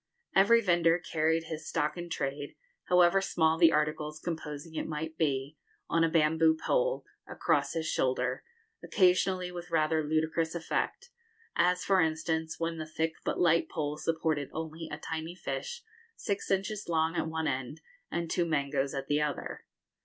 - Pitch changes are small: Yes, narrow, 2.1 semitones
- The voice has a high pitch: No, medium, 160 Hz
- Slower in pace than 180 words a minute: Yes, average, 160 wpm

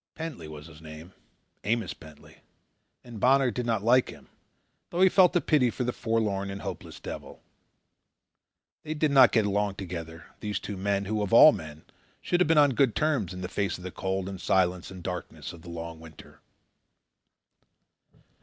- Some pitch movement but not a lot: No, wide, 6.0 semitones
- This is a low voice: Yes, low, 100 Hz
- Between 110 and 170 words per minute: No, average, 180 wpm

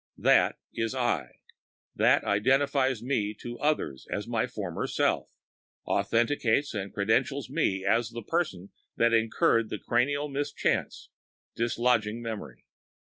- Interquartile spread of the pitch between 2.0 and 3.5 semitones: No, average, 4.2 semitones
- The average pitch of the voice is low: Yes, low, 115 Hz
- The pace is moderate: No, slow, 105 wpm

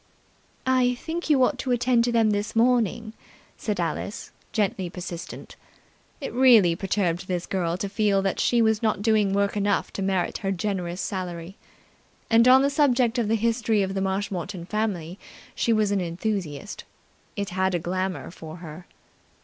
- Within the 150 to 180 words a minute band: Yes, average, 165 wpm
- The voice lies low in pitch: No, high, 200 Hz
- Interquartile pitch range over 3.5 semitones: Yes, average, 3.9 semitones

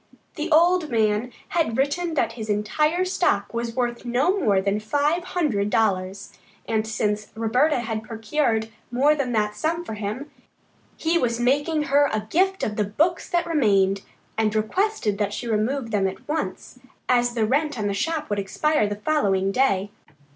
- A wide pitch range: Yes, wide, 6.4 semitones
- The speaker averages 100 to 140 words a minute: No, average, 170 wpm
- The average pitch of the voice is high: Yes, high, 235 Hz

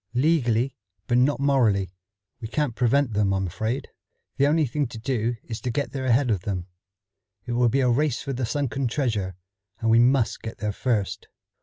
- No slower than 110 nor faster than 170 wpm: No, average, 190 wpm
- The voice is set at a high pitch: No, low, 120 Hz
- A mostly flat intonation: No, average, 3.7 semitones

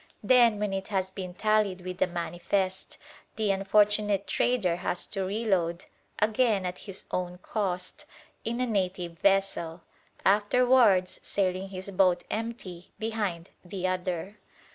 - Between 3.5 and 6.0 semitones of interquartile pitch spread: No, narrow, 2.6 semitones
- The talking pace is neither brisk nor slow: No, slow, 130 wpm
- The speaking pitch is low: No, high, 195 Hz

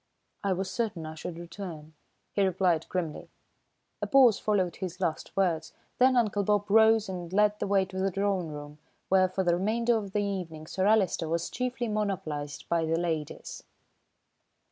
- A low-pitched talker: No, high, 190 Hz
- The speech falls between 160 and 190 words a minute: Yes, average, 170 wpm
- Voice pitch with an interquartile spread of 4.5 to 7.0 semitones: No, average, 3.7 semitones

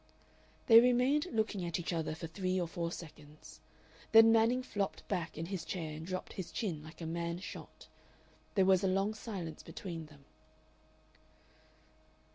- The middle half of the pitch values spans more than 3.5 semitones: Yes, average, 4.4 semitones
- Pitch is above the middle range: No, medium, 180 Hz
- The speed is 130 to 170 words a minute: Yes, average, 160 wpm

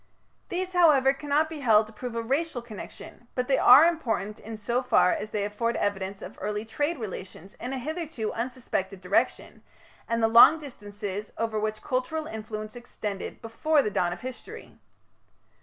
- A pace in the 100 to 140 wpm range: No, average, 170 wpm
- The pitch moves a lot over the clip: No, average, 4.7 semitones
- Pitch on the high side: Yes, high, 230 Hz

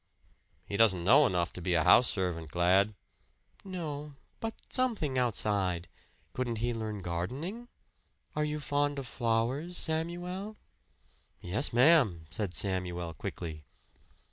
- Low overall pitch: Yes, low, 115 Hz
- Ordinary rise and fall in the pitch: No, wide, 8.8 semitones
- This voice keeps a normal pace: No, slow, 125 wpm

